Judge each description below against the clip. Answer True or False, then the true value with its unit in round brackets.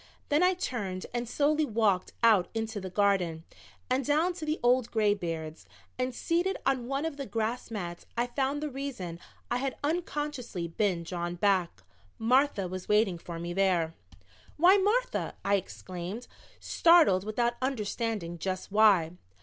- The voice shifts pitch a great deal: True (6.9 semitones)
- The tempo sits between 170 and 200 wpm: False (150 wpm)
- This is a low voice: False (225 Hz)